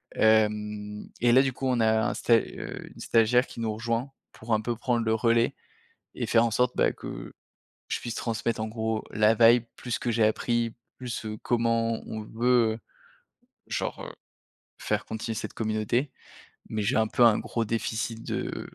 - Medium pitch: No, low, 115 Hz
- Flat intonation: Yes, narrow, 1.4 semitones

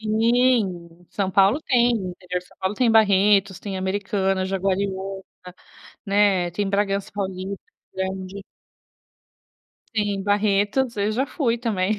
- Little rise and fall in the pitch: Yes, narrow, 2.1 semitones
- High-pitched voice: Yes, high, 200 Hz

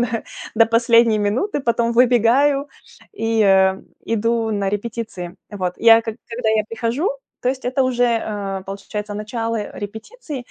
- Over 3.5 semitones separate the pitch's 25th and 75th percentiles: No, narrow, 2.5 semitones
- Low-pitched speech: No, high, 230 Hz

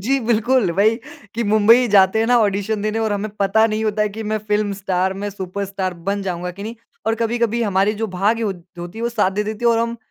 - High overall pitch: Yes, high, 215 Hz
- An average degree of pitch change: No, narrow, 2.3 semitones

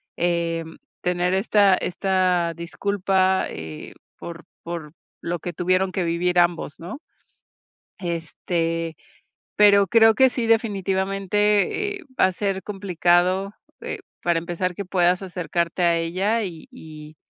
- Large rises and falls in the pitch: No, narrow, 2.6 semitones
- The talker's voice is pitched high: No, medium, 180 Hz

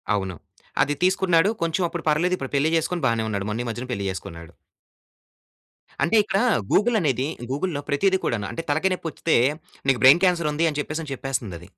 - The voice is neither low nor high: Yes, medium, 145 Hz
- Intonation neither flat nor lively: No, wide, 6.4 semitones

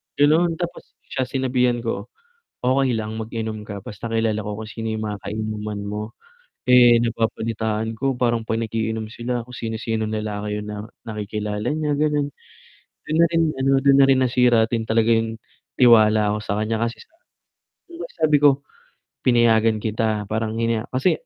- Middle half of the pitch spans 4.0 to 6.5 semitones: No, narrow, 2.6 semitones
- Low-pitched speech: Yes, low, 115 Hz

